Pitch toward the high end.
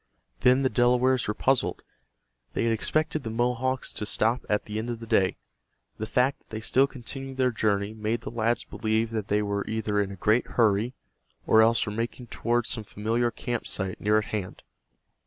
No: low, 115 Hz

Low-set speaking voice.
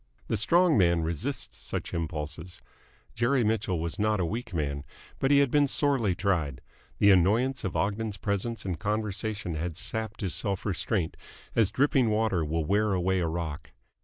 Yes: low, 100 Hz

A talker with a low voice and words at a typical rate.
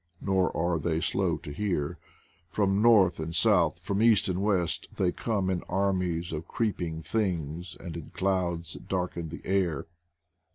Yes: very low, 90 Hz; average, 165 wpm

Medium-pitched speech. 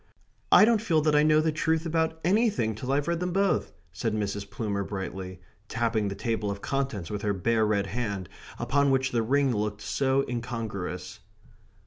No: low, 115 Hz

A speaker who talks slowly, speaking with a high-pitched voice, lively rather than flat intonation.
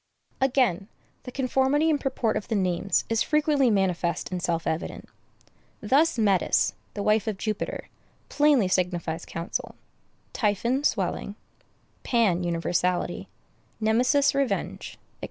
Yes: slow, 120 wpm; high, 215 Hz; wide, 6.5 semitones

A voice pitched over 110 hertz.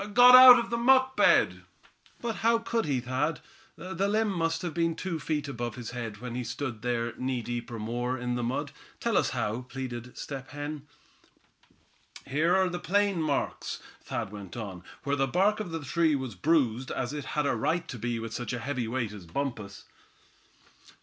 Yes: low, 135 Hz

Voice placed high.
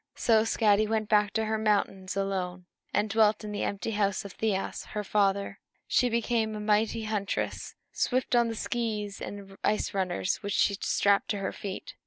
Yes: high, 210 Hz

